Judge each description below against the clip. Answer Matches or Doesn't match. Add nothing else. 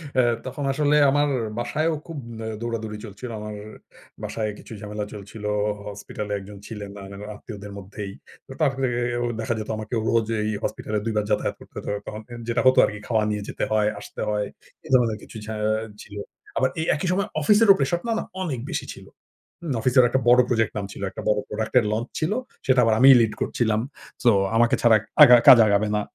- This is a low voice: Matches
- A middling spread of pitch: Matches